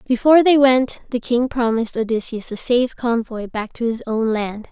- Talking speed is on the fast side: No, average, 190 wpm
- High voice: Yes, high, 240 Hz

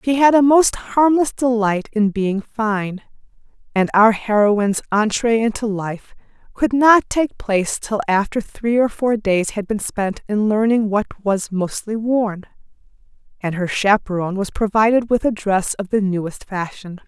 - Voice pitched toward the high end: Yes, high, 215 Hz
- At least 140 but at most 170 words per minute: Yes, average, 160 wpm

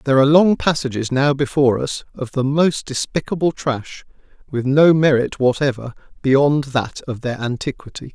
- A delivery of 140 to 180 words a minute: Yes, average, 155 wpm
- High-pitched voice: No, low, 135 Hz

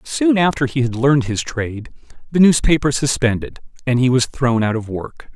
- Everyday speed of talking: Yes, average, 190 wpm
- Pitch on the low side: Yes, low, 130 Hz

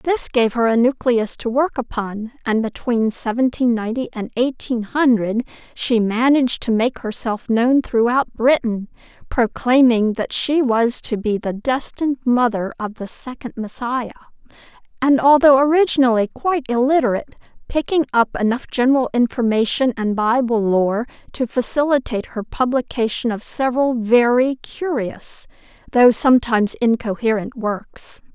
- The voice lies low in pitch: No, high, 240 Hz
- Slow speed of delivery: Yes, slow, 130 wpm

